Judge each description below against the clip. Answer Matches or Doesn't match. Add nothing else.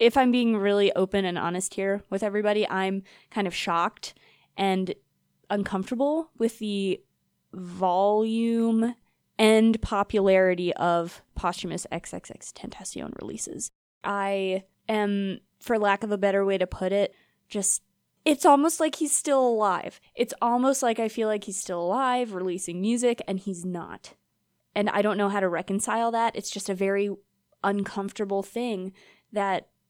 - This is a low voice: Doesn't match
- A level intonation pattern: Doesn't match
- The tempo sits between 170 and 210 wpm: Doesn't match